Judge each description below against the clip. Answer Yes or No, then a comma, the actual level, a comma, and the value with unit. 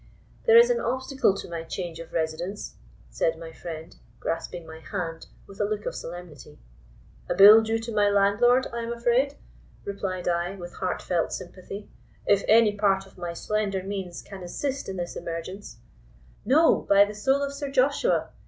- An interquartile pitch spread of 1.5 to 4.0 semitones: No, average, 4.8 semitones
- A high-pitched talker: Yes, high, 200 Hz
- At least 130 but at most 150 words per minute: No, average, 170 wpm